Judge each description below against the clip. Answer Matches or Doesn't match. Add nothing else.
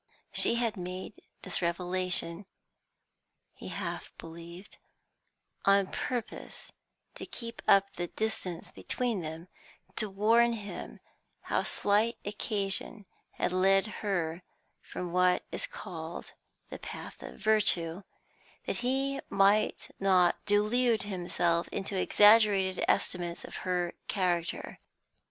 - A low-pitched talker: Doesn't match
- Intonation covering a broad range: Doesn't match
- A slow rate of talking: Matches